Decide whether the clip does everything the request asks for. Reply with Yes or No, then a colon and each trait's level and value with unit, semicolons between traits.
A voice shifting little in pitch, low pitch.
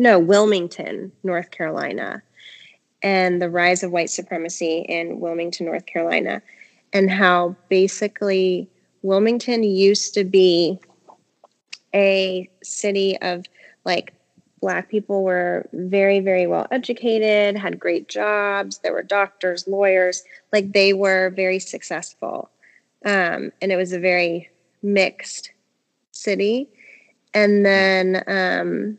No: narrow, 2.0 semitones; high, 190 Hz